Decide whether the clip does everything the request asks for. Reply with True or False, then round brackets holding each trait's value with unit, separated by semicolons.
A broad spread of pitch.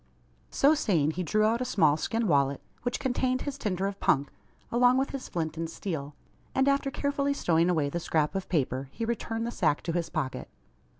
True (7.9 semitones)